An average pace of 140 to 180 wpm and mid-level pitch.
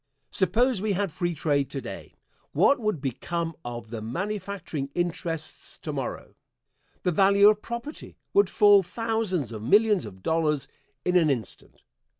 Yes: average, 150 wpm; medium, 175 Hz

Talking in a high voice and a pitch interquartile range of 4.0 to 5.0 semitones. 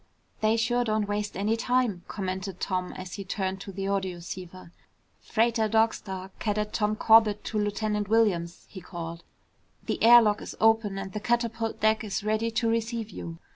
No: high, 210 Hz; average, 2.8 semitones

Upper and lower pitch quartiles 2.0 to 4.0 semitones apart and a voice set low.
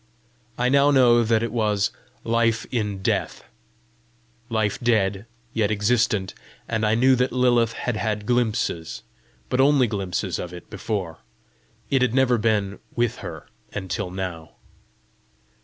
Yes: average, 3.3 semitones; low, 110 Hz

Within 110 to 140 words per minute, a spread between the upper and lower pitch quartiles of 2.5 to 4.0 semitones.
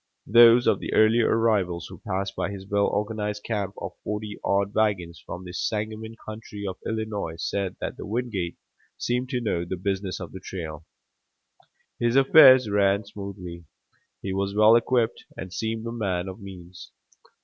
No: average, 160 wpm; average, 2.9 semitones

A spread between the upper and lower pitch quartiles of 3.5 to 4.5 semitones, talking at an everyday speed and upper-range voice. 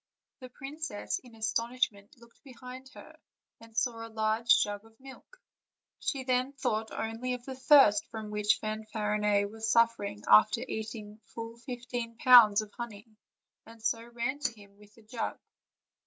No: narrow, 2.6 semitones; average, 160 wpm; high, 230 Hz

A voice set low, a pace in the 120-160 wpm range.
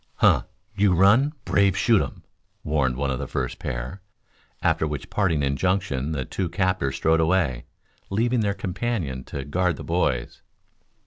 Yes: very low, 85 Hz; average, 150 wpm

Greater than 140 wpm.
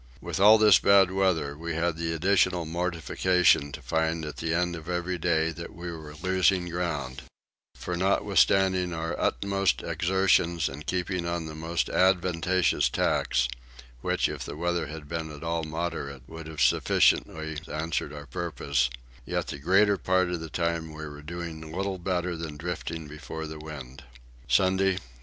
Yes: average, 165 wpm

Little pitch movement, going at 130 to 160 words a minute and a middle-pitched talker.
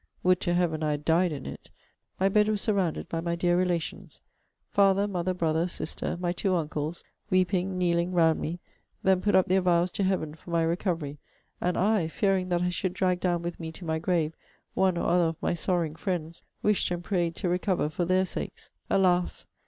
No: narrow, 2.0 semitones; average, 200 wpm; medium, 175 Hz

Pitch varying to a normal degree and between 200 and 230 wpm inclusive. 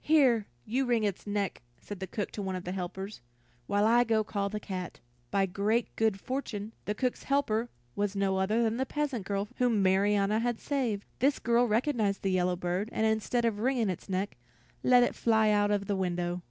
Yes: average, 3.2 semitones; fast, 205 wpm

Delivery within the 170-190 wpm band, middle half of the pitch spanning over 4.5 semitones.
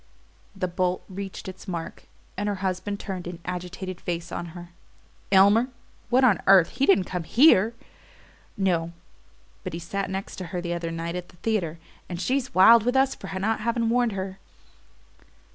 No: average, 175 wpm; average, 3.2 semitones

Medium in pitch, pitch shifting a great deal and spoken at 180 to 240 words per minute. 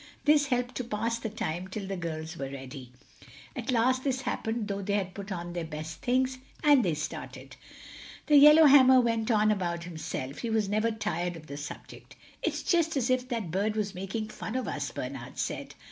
No: high, 215 Hz; wide, 6.4 semitones; average, 190 wpm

